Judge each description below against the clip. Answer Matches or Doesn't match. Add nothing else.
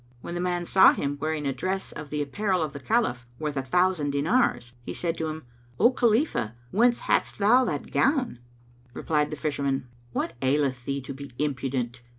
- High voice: Doesn't match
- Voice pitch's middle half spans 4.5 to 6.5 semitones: Matches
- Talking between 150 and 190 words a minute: Matches